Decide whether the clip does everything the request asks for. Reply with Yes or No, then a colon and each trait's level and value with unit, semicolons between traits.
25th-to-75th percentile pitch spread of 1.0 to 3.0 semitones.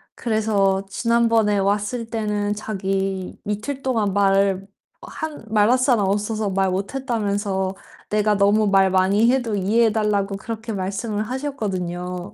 Yes: narrow, 2.4 semitones